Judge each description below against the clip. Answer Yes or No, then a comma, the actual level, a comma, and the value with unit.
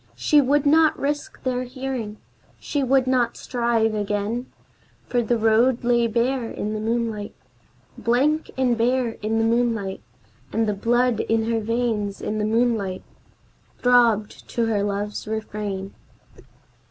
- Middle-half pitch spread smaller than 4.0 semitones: Yes, narrow, 2.6 semitones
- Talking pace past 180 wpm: No, average, 140 wpm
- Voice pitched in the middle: No, high, 230 Hz